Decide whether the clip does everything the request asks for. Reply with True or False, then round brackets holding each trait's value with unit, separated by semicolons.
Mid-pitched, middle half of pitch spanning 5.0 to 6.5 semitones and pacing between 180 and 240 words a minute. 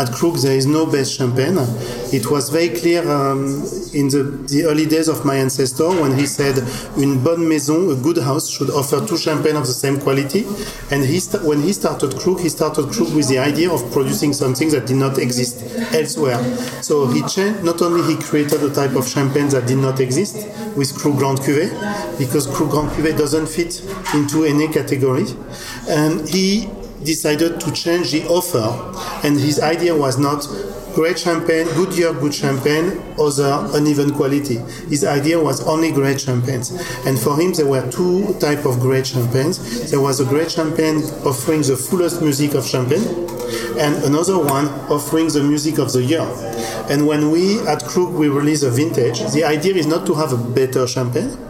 False (150 Hz; 3.1 semitones; 190 wpm)